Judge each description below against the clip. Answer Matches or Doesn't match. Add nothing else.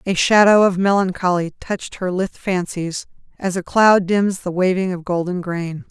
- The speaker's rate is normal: Matches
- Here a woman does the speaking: Matches